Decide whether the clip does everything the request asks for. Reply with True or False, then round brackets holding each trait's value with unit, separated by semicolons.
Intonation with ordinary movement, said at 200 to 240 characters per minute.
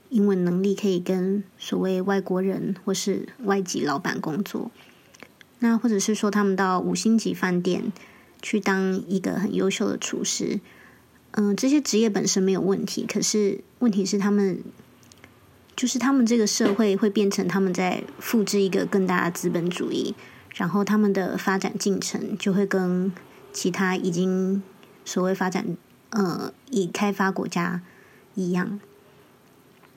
False (1.8 semitones; 230 characters per minute)